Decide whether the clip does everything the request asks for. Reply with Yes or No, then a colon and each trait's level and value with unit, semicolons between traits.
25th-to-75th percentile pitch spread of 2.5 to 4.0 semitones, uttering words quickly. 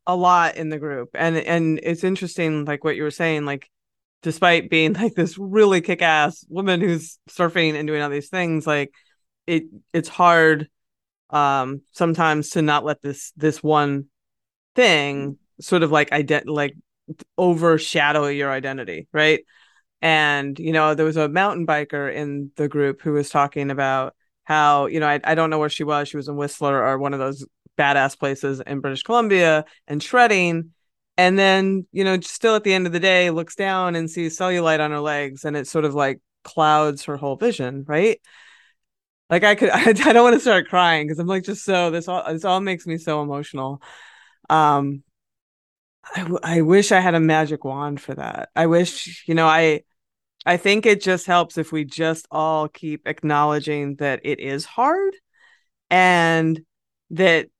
No: average, 3.4 semitones; average, 185 wpm